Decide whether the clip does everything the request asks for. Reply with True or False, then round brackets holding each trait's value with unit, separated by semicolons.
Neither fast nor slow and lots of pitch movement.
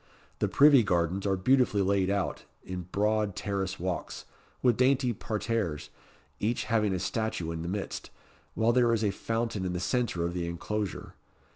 False (165 wpm; 3.8 semitones)